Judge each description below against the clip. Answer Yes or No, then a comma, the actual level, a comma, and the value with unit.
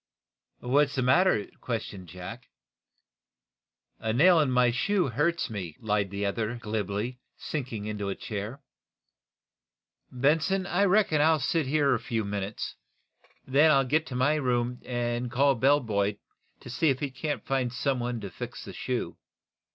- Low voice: Yes, low, 125 Hz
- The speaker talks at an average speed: Yes, average, 160 wpm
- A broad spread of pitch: No, average, 5.0 semitones